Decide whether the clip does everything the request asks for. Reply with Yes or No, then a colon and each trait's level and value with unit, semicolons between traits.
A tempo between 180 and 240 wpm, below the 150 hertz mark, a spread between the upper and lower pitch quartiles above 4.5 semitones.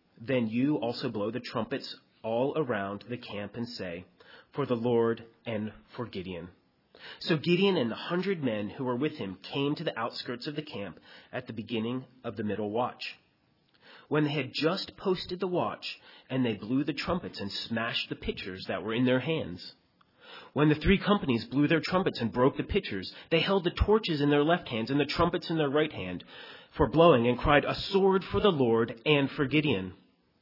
Yes: average, 200 wpm; low, 135 Hz; wide, 5.5 semitones